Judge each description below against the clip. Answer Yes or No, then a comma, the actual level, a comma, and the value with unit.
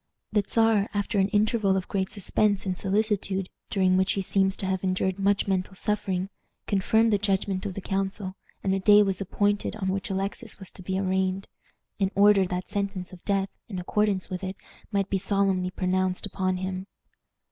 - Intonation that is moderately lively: No, narrow, 1.4 semitones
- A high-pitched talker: Yes, high, 195 Hz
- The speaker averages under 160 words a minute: No, average, 185 wpm